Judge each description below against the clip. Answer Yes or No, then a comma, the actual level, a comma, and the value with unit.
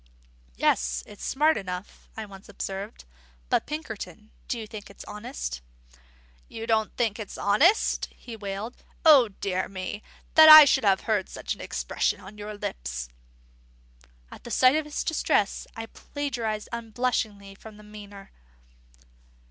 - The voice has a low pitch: No, high, 215 Hz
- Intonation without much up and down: No, average, 3.4 semitones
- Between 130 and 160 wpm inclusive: Yes, average, 140 wpm